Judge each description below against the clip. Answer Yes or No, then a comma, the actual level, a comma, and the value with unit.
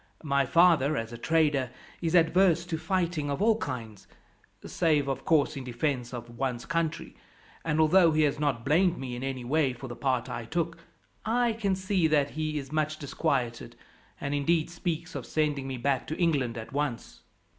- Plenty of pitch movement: No, average, 4.0 semitones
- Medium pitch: Yes, medium, 150 Hz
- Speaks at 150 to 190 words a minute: Yes, average, 185 wpm